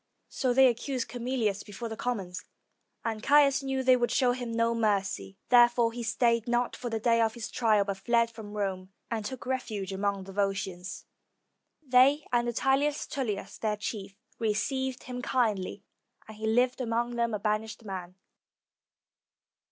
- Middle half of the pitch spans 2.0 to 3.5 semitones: Yes, average, 3.2 semitones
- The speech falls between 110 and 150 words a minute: No, average, 165 wpm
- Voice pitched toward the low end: No, high, 230 Hz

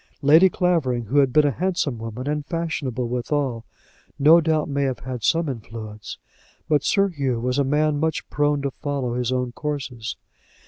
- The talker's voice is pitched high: No, medium, 140 Hz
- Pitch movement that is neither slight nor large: Yes, average, 3.5 semitones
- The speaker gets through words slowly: No, average, 175 wpm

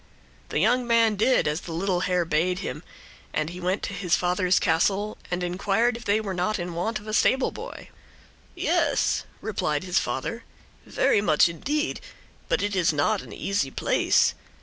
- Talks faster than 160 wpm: Yes, average, 170 wpm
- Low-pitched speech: No, medium, 185 Hz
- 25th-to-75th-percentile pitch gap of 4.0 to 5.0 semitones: No, average, 3.6 semitones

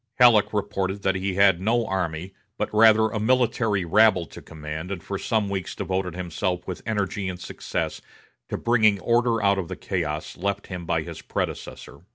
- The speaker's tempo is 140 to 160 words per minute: No, average, 180 wpm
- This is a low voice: Yes, low, 100 Hz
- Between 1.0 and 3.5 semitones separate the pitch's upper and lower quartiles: Yes, average, 3.1 semitones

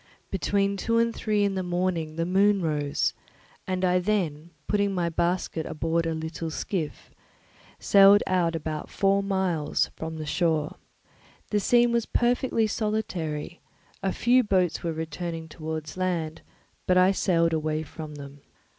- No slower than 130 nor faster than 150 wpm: Yes, average, 145 wpm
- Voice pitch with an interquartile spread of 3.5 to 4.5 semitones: Yes, average, 3.8 semitones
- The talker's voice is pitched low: No, medium, 175 Hz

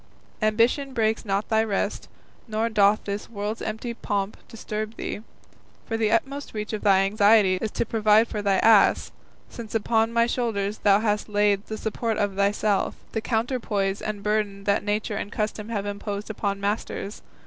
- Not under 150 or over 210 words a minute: Yes, average, 170 wpm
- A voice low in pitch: No, high, 210 Hz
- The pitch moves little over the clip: Yes, narrow, 1.7 semitones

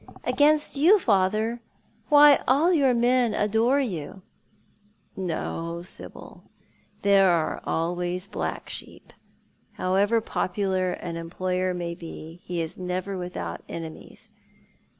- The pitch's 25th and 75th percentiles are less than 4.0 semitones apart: No, average, 5.2 semitones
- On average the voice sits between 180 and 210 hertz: Yes, medium, 185 Hz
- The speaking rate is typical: No, slow, 110 wpm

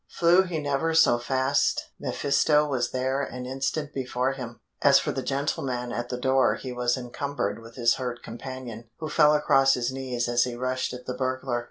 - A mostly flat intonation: Yes, narrow, 2.2 semitones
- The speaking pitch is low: Yes, low, 130 Hz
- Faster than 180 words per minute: Yes, average, 190 wpm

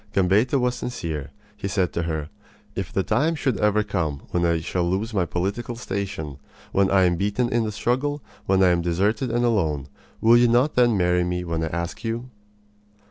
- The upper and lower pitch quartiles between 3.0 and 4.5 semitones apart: No, wide, 5.4 semitones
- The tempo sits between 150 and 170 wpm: No, average, 195 wpm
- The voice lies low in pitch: Yes, low, 100 Hz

